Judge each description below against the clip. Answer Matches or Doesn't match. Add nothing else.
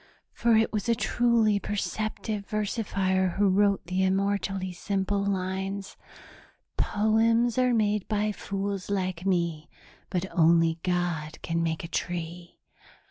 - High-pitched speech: Matches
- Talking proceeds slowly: Matches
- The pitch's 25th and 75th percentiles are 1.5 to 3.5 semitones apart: Matches